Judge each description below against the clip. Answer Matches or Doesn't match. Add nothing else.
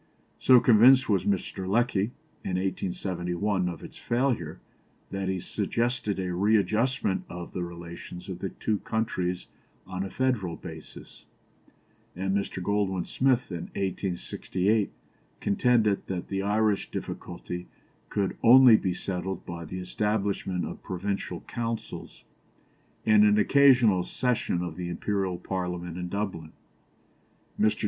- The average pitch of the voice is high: Doesn't match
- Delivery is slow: Matches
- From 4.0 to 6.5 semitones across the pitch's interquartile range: Doesn't match